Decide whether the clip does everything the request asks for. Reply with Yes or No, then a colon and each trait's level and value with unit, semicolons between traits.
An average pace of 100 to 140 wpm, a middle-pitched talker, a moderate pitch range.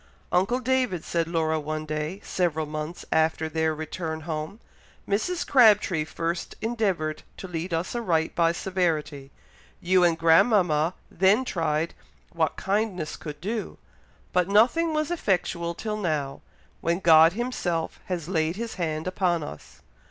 Yes: slow, 135 wpm; medium, 170 Hz; average, 3.9 semitones